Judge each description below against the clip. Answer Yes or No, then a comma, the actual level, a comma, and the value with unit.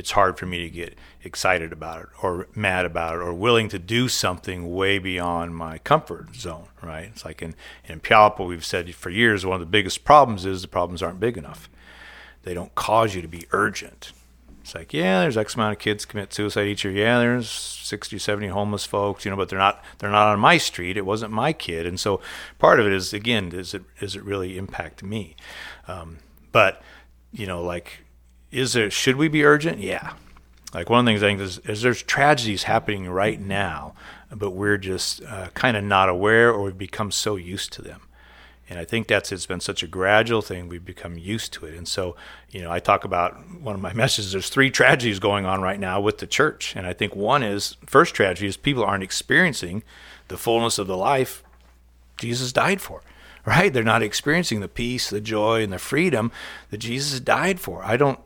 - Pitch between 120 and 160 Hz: No, low, 100 Hz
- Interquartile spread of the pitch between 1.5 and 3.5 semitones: No, average, 4.2 semitones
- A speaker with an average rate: No, fast, 215 wpm